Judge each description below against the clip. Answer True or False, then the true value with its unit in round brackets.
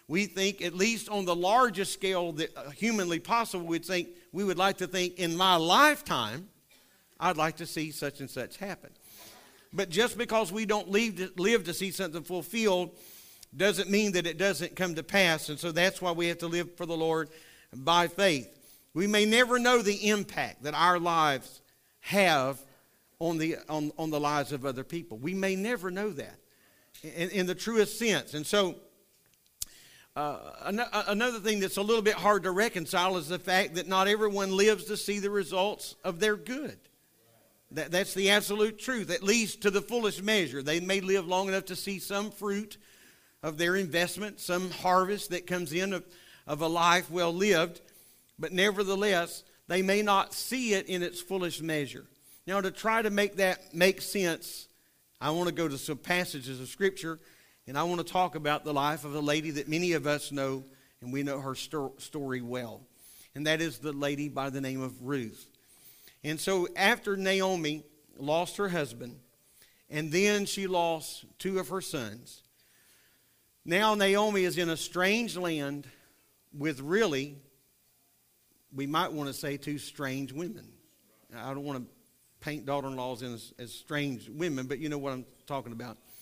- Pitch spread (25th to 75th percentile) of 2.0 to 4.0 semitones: False (4.8 semitones)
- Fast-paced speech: False (180 wpm)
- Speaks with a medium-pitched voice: True (175 Hz)